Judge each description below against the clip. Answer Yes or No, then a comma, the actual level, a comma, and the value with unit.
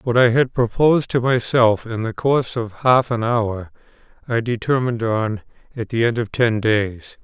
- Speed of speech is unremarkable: Yes, average, 180 wpm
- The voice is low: Yes, low, 115 Hz